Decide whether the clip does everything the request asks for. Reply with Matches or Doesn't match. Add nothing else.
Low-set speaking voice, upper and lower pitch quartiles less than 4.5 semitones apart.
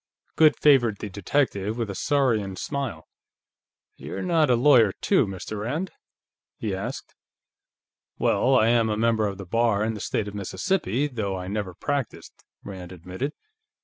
Doesn't match